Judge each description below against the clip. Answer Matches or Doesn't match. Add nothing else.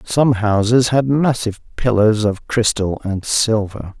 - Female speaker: Doesn't match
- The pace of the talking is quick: Doesn't match